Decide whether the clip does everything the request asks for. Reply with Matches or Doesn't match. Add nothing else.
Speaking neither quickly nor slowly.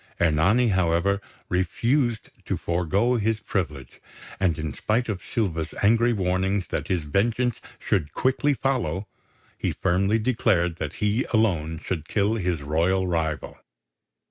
Doesn't match